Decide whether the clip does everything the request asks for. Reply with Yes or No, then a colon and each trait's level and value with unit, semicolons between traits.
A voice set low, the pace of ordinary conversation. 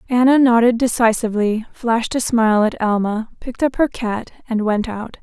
No: high, 230 Hz; average, 170 wpm